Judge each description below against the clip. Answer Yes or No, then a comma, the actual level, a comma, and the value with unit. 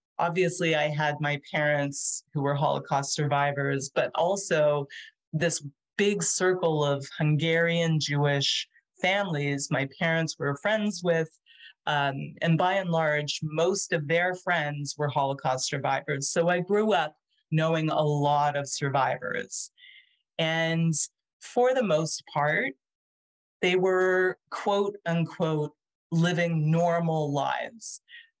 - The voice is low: No, medium, 160 Hz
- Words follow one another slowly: Yes, slow, 120 wpm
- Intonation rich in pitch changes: No, average, 3.7 semitones